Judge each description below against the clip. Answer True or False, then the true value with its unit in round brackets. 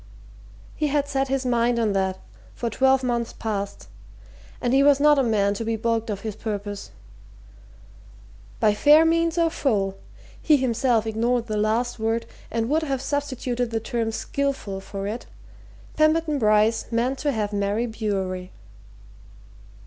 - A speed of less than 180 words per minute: True (150 wpm)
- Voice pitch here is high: True (230 Hz)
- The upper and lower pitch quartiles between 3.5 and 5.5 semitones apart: True (4.2 semitones)